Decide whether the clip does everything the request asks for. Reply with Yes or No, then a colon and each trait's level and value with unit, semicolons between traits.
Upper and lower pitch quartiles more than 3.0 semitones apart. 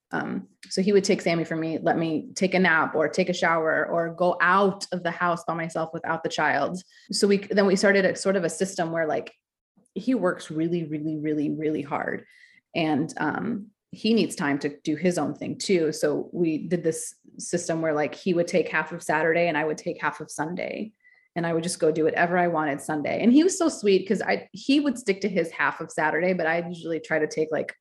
Yes: average, 3.6 semitones